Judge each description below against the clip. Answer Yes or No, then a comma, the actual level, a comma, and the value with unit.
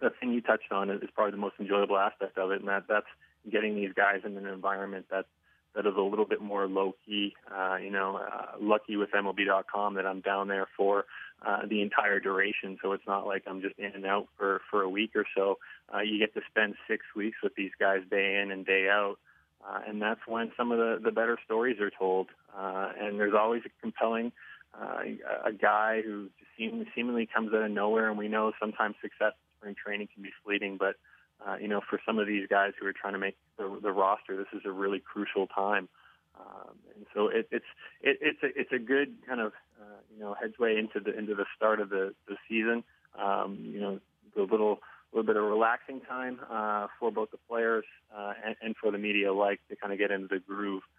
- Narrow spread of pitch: Yes, narrow, 1.6 semitones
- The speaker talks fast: Yes, fast, 225 wpm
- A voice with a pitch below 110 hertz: Yes, low, 100 Hz